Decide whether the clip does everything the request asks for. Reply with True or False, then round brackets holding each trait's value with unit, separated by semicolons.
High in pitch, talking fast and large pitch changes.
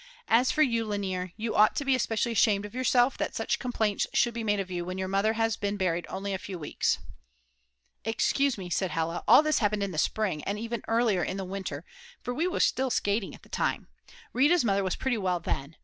False (205 Hz; 225 wpm; 3.9 semitones)